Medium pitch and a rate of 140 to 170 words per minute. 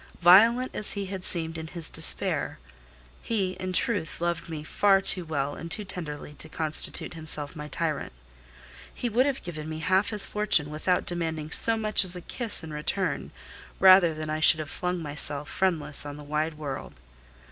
No: medium, 165 Hz; average, 180 wpm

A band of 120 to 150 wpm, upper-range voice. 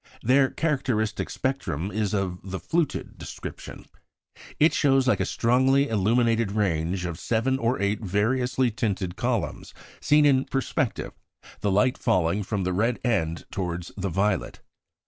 No: average, 140 wpm; low, 110 Hz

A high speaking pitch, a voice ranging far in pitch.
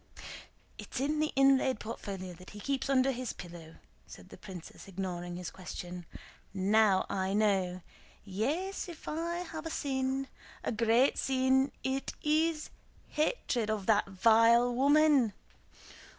Yes: high, 235 Hz; wide, 6.2 semitones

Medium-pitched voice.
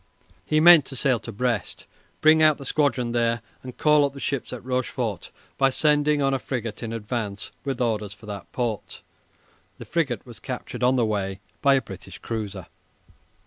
No: low, 125 Hz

